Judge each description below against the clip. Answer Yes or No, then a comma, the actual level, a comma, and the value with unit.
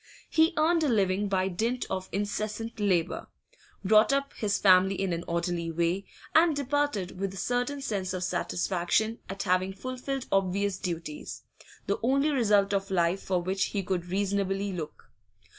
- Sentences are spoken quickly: No, average, 160 wpm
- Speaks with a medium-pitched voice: No, high, 195 Hz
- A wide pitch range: No, average, 3.9 semitones